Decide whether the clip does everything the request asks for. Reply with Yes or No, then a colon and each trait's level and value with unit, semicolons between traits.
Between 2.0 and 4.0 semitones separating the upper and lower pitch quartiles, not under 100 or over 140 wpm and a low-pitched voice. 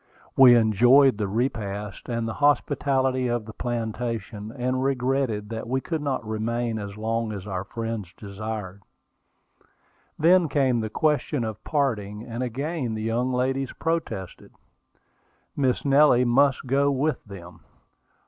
Yes: average, 3.7 semitones; slow, 135 wpm; low, 120 Hz